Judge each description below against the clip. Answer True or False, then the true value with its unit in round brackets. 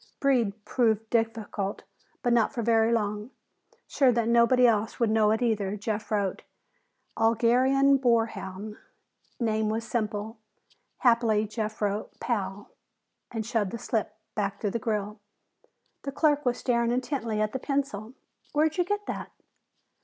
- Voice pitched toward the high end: True (225 Hz)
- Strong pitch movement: False (2.4 semitones)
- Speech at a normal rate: True (145 wpm)